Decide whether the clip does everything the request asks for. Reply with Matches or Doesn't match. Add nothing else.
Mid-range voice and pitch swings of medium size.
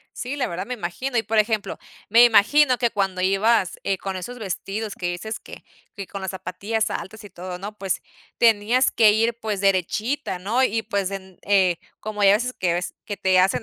Doesn't match